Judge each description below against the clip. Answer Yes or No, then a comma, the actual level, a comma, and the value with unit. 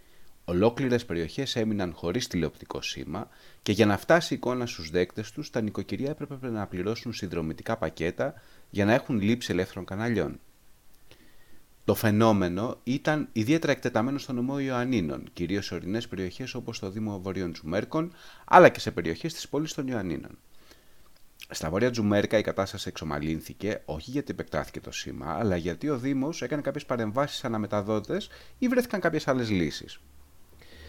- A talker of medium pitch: No, low, 110 Hz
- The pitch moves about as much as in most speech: No, wide, 6.4 semitones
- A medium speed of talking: Yes, average, 150 wpm